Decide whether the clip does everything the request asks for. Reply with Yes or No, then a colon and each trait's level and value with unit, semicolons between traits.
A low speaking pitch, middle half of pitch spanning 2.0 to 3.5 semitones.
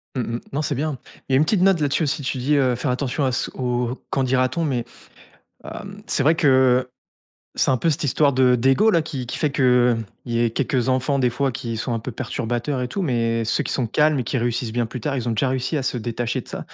Yes: low, 130 Hz; average, 2.7 semitones